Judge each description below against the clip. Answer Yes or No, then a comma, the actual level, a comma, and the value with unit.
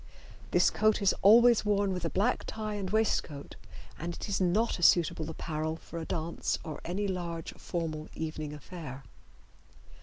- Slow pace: No, average, 160 wpm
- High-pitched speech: No, medium, 175 Hz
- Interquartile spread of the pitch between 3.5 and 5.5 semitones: Yes, average, 4.2 semitones